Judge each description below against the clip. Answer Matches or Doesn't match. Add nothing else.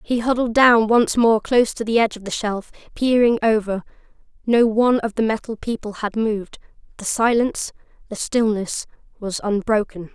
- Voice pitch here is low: Doesn't match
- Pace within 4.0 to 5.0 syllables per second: Doesn't match